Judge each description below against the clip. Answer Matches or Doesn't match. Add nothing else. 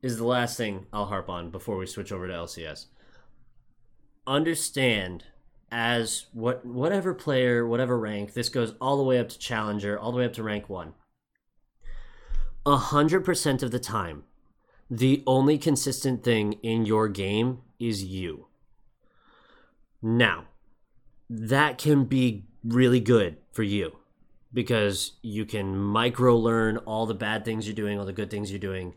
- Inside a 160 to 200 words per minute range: Doesn't match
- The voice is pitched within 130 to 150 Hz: Doesn't match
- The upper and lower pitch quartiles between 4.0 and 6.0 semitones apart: Doesn't match